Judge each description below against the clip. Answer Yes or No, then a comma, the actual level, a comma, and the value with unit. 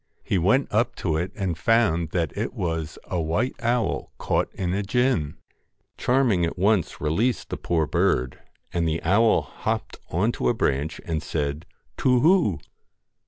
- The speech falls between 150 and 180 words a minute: Yes, average, 165 wpm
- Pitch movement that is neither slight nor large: No, wide, 6.3 semitones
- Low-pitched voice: Yes, very low, 90 Hz